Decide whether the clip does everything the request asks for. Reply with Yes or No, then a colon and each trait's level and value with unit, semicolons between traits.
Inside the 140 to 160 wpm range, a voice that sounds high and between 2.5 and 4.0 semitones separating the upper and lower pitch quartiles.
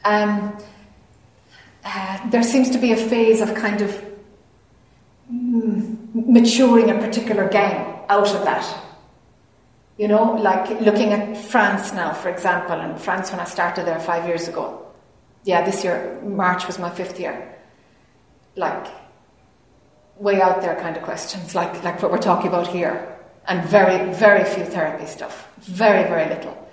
Yes: average, 155 wpm; high, 200 Hz; average, 3.4 semitones